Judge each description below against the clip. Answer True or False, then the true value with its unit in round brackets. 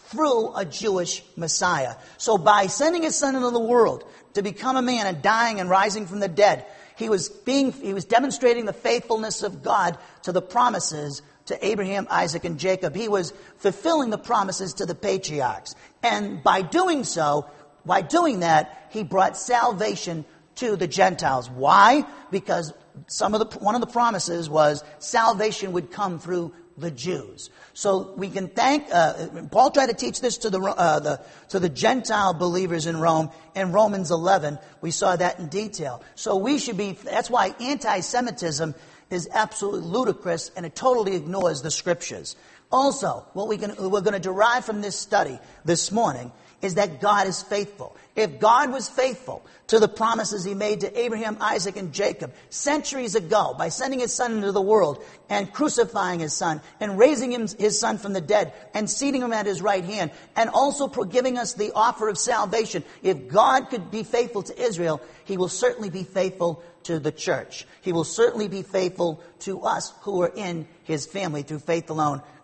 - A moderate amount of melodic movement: True (4.6 semitones)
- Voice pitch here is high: True (200 Hz)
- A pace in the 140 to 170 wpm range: False (180 wpm)